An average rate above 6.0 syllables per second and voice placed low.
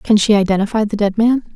No: 6.2 syllables/s; high, 210 Hz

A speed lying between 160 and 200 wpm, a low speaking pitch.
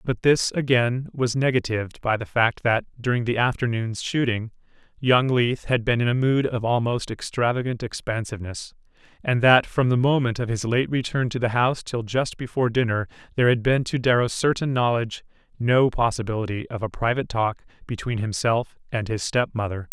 Yes: average, 180 wpm; low, 120 Hz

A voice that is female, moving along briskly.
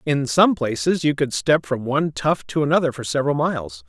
No: male; fast, 215 wpm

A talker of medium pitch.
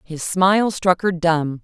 Yes: medium, 175 Hz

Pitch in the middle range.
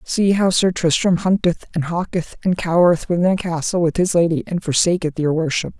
Yes: medium, 175 Hz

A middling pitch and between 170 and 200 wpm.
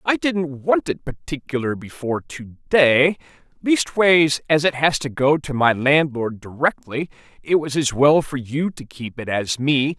Yes: medium, 145 Hz; average, 175 wpm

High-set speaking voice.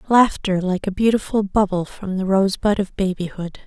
Yes: high, 195 Hz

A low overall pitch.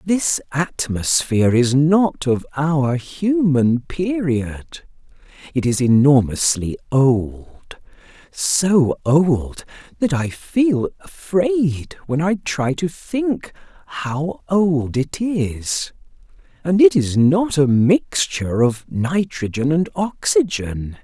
No: medium, 155 Hz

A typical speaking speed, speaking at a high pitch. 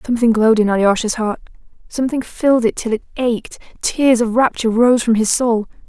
Yes: average, 185 wpm; high, 230 Hz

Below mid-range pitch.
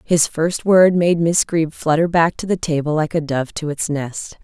No: medium, 160 Hz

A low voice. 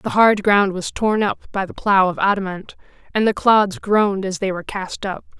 No: high, 200 Hz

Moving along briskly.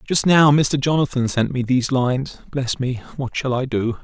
No: average, 195 wpm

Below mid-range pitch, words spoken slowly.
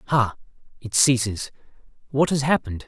Yes: low, 125 Hz; slow, 105 wpm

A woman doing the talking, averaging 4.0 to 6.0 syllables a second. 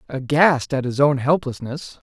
No: male; 4.3 syllables/s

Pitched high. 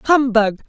Yes: high, 240 Hz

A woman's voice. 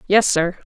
Yes: female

